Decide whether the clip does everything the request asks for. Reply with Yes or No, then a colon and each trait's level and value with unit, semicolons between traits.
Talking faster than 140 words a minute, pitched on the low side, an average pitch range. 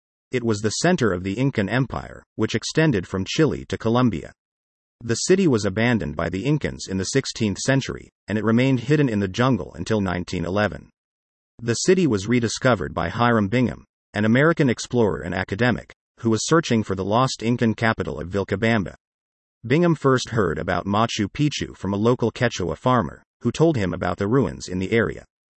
Yes: average, 180 wpm; low, 110 Hz; average, 4.7 semitones